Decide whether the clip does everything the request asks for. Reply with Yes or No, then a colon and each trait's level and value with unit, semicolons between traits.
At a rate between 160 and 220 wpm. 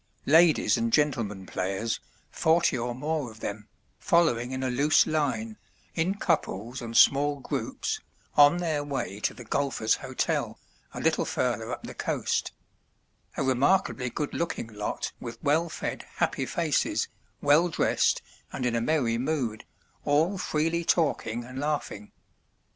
No: average, 140 wpm